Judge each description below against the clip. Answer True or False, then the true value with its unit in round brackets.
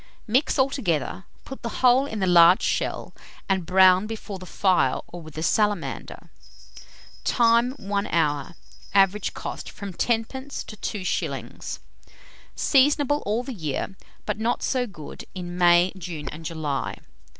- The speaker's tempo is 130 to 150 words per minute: True (140 wpm)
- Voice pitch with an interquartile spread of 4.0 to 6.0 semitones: True (5.4 semitones)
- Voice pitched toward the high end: True (195 Hz)